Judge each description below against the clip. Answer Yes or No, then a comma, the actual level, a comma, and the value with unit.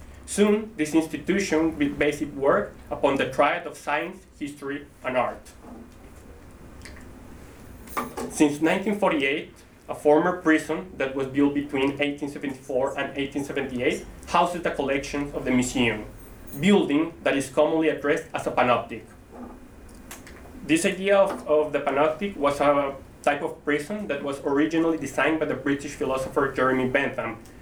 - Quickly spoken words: No, slow, 135 wpm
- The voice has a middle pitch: Yes, medium, 145 Hz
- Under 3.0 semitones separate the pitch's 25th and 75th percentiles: Yes, narrow, 2.5 semitones